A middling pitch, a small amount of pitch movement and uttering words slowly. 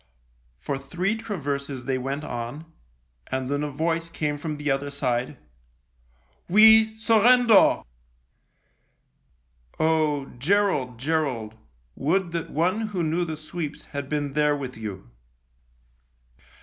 No: medium, 150 Hz; average, 4.3 semitones; slow, 120 wpm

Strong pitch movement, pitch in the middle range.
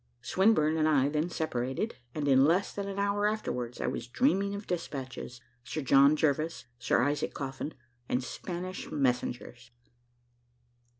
Yes: wide, 5.9 semitones; medium, 155 Hz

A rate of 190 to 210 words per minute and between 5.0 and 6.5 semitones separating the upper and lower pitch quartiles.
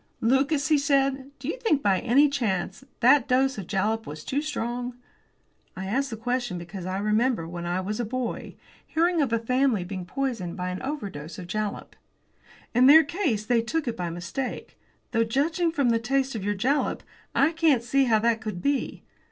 Yes: average, 195 wpm; average, 5.3 semitones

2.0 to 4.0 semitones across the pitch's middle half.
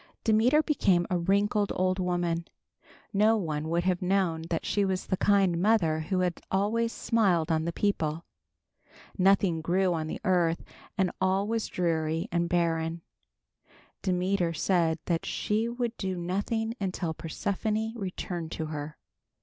Yes: average, 3.3 semitones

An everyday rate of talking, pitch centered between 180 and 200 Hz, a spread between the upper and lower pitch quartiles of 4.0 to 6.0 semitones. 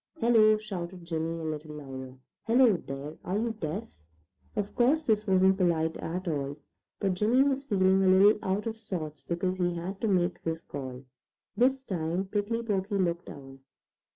Yes: average, 175 wpm; medium, 185 Hz; average, 4.7 semitones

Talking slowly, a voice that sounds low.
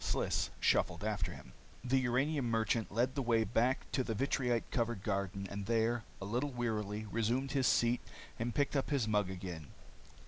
No: average, 175 wpm; low, 115 Hz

